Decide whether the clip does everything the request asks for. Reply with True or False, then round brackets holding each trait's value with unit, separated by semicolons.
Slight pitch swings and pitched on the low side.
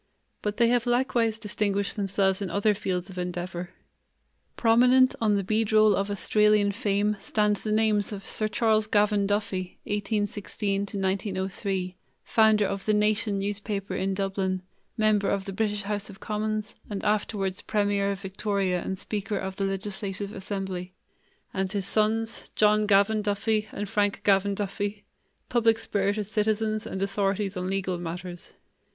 False (1.7 semitones; 205 Hz)